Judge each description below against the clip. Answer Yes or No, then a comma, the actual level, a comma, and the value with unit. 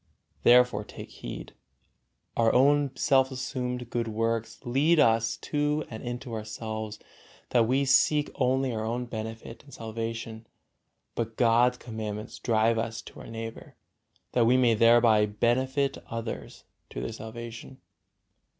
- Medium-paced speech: No, slow, 130 wpm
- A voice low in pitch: Yes, low, 115 Hz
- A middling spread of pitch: No, narrow, 2.2 semitones